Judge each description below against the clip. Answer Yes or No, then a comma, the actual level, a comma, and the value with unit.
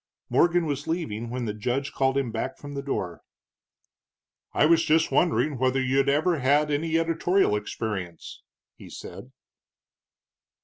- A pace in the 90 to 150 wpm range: Yes, average, 140 wpm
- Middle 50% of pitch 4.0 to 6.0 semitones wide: Yes, average, 4.6 semitones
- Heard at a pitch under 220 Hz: Yes, medium, 140 Hz